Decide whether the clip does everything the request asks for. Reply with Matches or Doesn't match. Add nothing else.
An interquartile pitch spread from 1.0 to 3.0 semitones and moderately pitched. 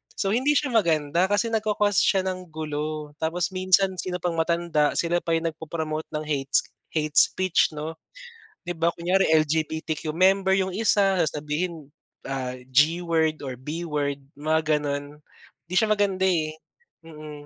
Doesn't match